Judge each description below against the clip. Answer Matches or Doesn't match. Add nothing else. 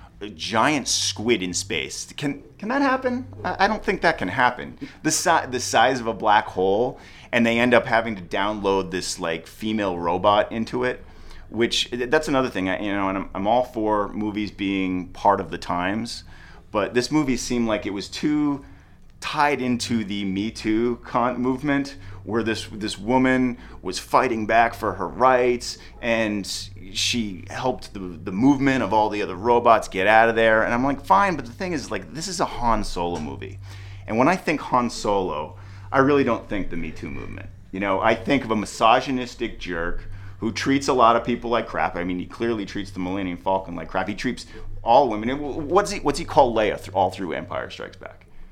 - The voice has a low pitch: Matches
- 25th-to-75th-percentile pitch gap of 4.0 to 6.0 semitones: Matches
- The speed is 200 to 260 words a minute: Matches